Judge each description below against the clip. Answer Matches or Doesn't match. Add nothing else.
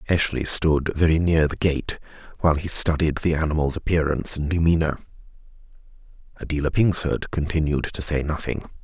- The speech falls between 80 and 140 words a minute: Matches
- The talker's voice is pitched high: Doesn't match